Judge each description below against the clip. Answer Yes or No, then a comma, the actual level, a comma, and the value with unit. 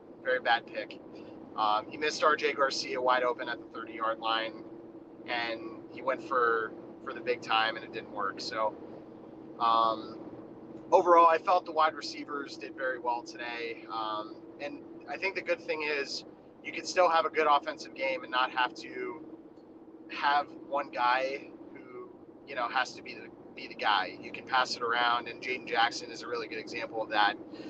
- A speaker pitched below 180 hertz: Yes, low, 135 Hz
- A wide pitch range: Yes, wide, 6.7 semitones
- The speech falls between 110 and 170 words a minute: No, average, 185 wpm